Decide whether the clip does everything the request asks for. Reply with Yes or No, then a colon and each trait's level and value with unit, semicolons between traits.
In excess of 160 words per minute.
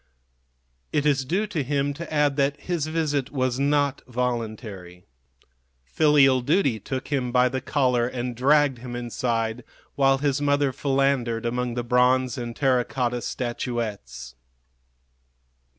No: slow, 135 wpm